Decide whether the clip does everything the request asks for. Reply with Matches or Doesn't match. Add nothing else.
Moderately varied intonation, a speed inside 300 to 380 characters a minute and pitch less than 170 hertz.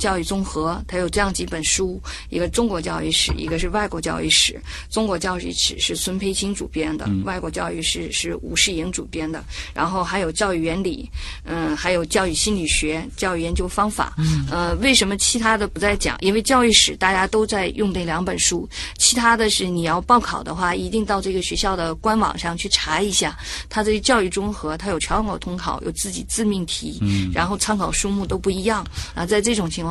Doesn't match